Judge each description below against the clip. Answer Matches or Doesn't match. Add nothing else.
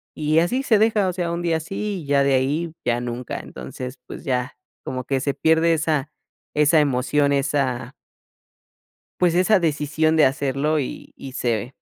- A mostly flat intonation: Doesn't match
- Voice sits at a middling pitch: Matches